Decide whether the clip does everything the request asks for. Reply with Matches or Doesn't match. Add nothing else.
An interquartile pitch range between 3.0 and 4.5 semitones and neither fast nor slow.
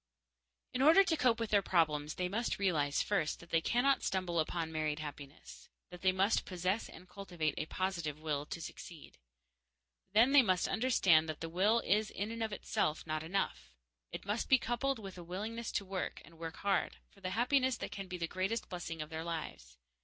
Doesn't match